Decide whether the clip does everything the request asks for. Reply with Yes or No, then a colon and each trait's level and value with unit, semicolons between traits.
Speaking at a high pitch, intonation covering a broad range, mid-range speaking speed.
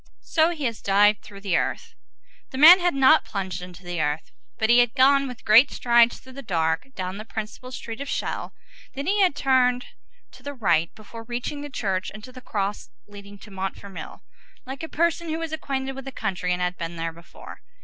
No: high, 235 Hz; wide, 5.9 semitones; fast, 210 wpm